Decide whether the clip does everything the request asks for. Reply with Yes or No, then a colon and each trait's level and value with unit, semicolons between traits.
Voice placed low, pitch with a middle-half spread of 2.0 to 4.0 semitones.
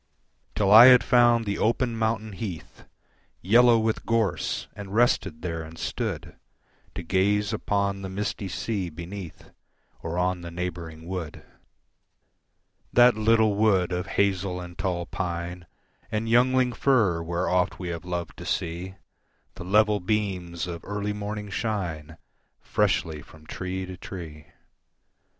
Yes: very low, 95 Hz; average, 3.7 semitones